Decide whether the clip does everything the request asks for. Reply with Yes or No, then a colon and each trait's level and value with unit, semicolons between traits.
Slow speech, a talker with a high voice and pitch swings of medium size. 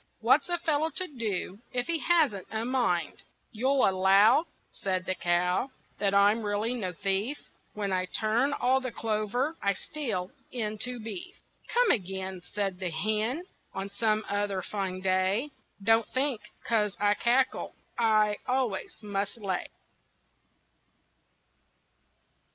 Yes: slow, 130 wpm; high, 215 Hz; average, 4.5 semitones